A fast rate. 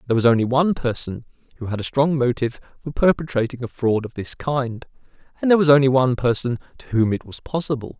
Yes: fast, 210 wpm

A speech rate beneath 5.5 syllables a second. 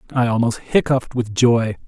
Yes: 5.3 syllables/s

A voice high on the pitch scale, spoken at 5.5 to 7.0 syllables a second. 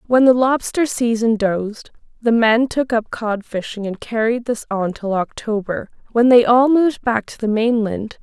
No: high, 230 Hz; 4.6 syllables/s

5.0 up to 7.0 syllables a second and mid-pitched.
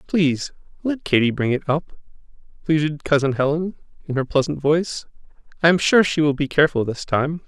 Yes: 5.6 syllables/s; medium, 150 Hz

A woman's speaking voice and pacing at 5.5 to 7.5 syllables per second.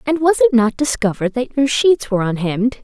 Yes: female; 6.0 syllables/s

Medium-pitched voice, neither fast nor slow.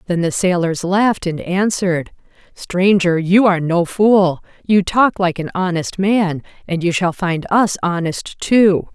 Yes: medium, 180 Hz; average, 160 wpm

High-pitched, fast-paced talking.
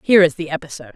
No: medium, 165 Hz; fast, 250 wpm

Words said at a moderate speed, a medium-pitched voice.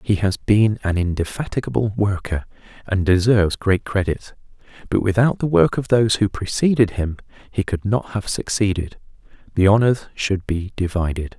No: average, 155 wpm; low, 100 Hz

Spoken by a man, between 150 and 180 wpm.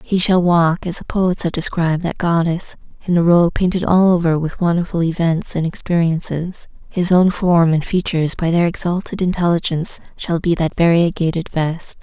No: female; average, 170 wpm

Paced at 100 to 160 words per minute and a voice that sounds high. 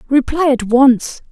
Yes: slow, 135 wpm; very high, 260 Hz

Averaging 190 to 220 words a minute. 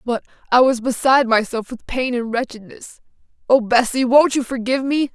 No: average, 175 wpm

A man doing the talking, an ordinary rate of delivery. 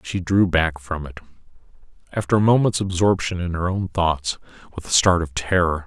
Yes: male; average, 185 wpm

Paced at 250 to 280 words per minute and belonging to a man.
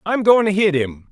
Yes: fast, 270 wpm; male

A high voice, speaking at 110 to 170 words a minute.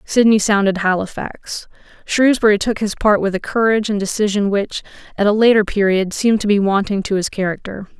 No: high, 205 Hz; average, 180 wpm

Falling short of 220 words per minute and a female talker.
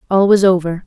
Yes: fast, 205 wpm; female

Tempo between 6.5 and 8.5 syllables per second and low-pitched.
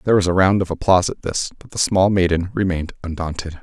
Yes: 6.6 syllables/s; very low, 90 Hz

